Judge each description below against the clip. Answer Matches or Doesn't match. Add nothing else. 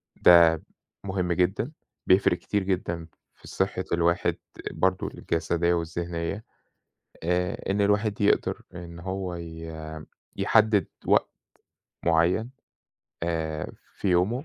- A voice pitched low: Matches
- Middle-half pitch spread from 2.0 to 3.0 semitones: Matches